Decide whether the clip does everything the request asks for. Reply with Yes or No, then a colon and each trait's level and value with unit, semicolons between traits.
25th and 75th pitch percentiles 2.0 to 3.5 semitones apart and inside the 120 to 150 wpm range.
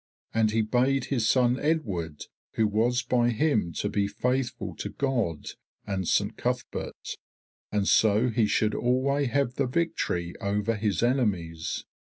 No: average, 4.0 semitones; average, 145 wpm